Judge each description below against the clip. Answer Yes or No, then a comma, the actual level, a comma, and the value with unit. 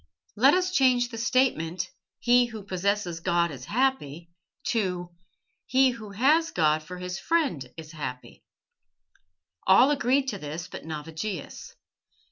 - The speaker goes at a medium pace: No, slow, 130 wpm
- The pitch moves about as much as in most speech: No, wide, 7.6 semitones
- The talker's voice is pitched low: No, high, 200 Hz